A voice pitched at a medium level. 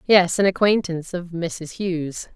Yes: medium, 175 Hz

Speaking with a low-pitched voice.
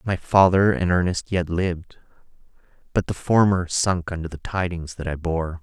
Yes: very low, 90 Hz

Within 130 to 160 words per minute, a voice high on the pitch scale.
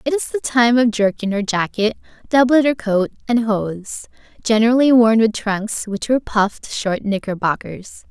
Yes: average, 155 wpm; high, 225 Hz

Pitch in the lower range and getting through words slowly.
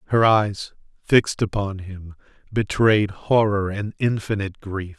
Yes: low, 100 Hz; slow, 120 wpm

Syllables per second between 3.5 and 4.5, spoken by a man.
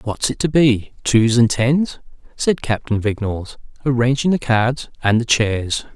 Yes: 4.2 syllables/s; male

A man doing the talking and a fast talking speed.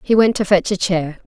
No: female; fast, 280 wpm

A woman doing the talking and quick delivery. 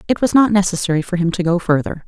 Yes: female; fast, 260 wpm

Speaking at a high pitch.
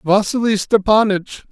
Yes: high, 205 Hz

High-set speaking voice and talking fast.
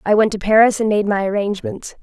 Yes: high, 210 Hz; fast, 235 wpm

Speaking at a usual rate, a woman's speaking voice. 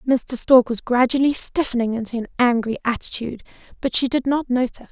Yes: average, 170 wpm; female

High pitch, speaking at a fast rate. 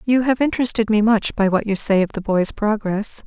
Yes: high, 215 Hz; fast, 240 wpm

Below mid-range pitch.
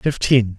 Yes: low, 115 Hz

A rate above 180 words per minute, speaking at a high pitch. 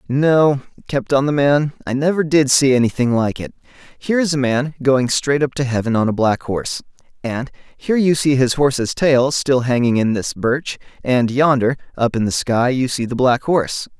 No: average, 200 wpm; low, 135 Hz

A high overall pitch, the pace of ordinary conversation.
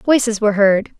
Yes: high, 215 Hz; average, 180 wpm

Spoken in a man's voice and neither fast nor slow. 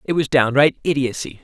Yes: male; average, 165 wpm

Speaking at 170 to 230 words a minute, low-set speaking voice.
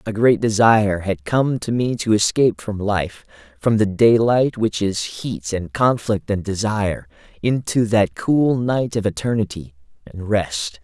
No: average, 155 wpm; low, 105 Hz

